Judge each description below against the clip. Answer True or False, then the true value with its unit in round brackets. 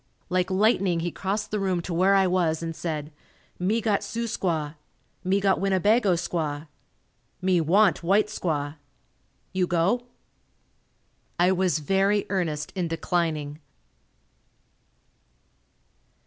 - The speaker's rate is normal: False (120 wpm)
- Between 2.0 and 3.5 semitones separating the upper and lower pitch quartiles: True (3.0 semitones)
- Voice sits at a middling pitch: True (180 Hz)